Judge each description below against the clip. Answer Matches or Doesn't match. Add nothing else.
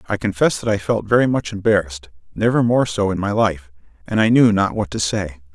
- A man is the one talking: Matches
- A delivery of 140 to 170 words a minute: Doesn't match